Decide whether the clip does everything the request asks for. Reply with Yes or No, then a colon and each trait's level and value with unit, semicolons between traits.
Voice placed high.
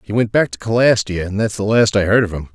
No: low, 105 Hz